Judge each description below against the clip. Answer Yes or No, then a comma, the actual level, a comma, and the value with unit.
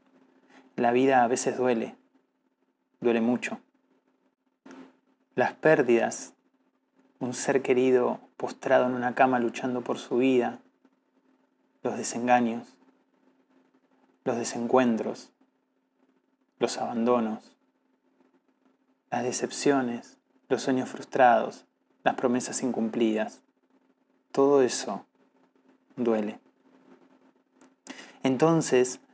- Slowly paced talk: Yes, slow, 80 wpm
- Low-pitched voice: Yes, low, 125 Hz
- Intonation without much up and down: Yes, narrow, 1.9 semitones